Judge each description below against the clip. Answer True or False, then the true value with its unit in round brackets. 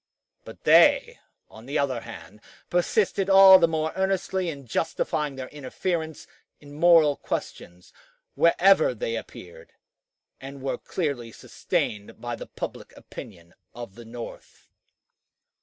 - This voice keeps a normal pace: False (125 wpm)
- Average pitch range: False (6.5 semitones)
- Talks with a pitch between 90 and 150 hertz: True (140 Hz)